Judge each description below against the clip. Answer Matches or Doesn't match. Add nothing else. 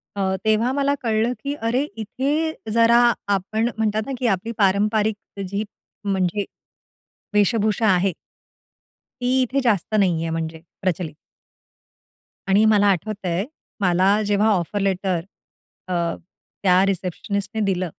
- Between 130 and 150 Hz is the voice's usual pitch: Doesn't match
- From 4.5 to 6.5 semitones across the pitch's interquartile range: Doesn't match